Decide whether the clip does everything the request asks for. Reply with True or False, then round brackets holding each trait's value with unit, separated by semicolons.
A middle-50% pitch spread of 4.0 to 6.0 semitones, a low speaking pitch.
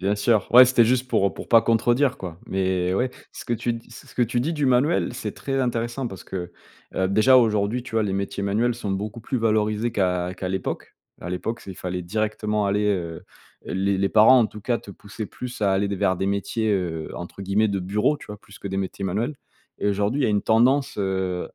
False (3.6 semitones; 105 Hz)